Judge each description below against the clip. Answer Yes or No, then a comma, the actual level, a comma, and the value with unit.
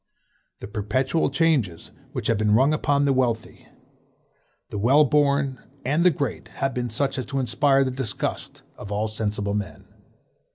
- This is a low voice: Yes, low, 130 Hz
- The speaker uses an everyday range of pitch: Yes, average, 4.6 semitones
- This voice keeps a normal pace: Yes, average, 160 wpm